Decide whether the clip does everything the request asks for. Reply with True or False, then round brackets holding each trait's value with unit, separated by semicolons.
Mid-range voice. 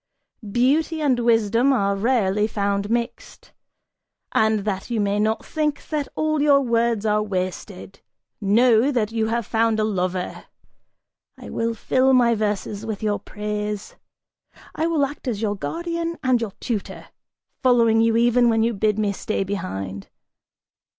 False (225 Hz)